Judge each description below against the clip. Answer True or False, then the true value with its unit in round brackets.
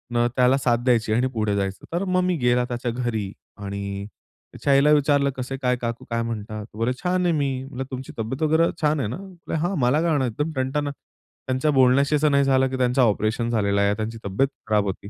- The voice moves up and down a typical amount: True (4.0 semitones)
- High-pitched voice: False (125 Hz)